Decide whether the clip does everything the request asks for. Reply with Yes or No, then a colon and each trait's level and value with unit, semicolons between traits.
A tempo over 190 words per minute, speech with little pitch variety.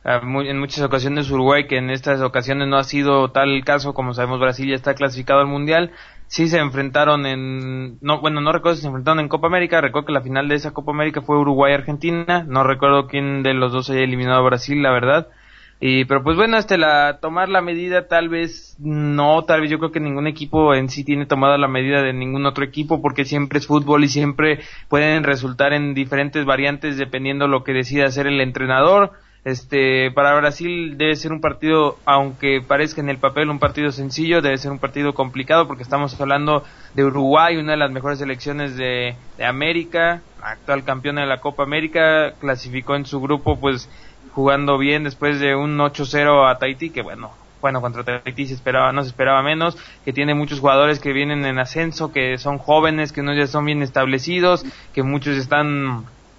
Yes: fast, 205 wpm; narrow, 1.9 semitones